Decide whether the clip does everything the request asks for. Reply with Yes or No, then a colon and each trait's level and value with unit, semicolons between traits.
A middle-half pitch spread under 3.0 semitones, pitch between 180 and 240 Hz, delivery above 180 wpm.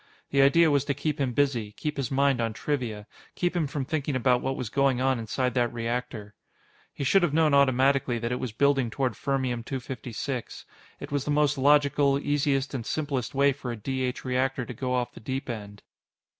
No: narrow, 2.5 semitones; low, 135 Hz; fast, 205 wpm